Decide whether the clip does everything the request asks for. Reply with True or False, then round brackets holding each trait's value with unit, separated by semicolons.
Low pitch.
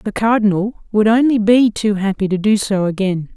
False (210 Hz)